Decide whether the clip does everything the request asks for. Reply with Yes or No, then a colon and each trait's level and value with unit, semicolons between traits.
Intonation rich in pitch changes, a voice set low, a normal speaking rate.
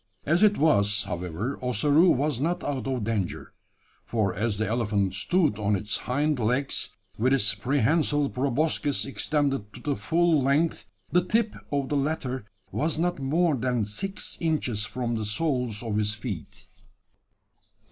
Yes: wide, 6.0 semitones; low, 130 Hz; average, 150 wpm